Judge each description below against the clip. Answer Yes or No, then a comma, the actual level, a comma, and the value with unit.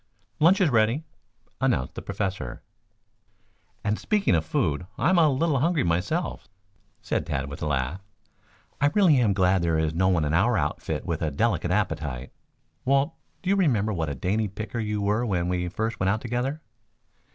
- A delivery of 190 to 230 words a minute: No, average, 175 wpm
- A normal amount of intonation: No, wide, 8.2 semitones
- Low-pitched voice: Yes, low, 100 Hz